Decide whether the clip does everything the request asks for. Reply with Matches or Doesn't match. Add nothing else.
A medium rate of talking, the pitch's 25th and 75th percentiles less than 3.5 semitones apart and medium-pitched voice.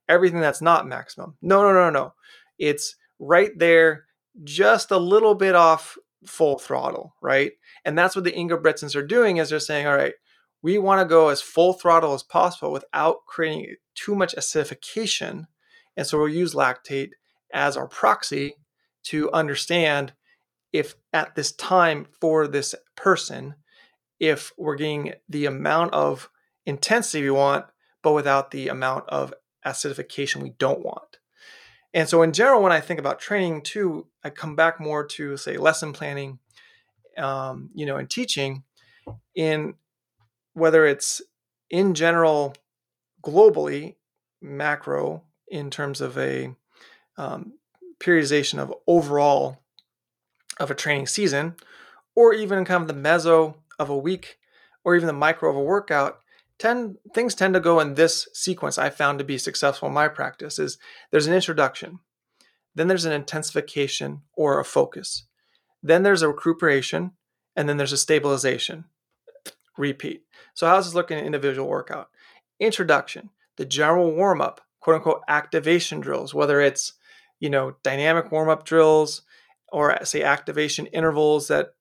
Doesn't match